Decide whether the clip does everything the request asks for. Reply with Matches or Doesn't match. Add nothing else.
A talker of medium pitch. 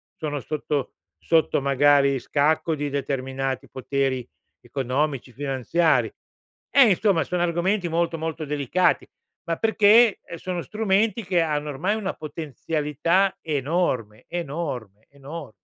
Matches